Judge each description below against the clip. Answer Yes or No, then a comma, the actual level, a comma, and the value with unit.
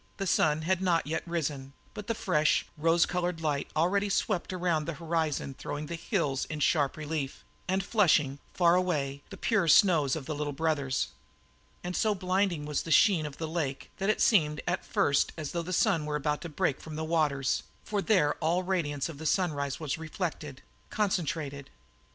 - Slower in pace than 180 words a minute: No, average, 185 wpm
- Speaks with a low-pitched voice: No, medium, 160 Hz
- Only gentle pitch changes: No, average, 3.5 semitones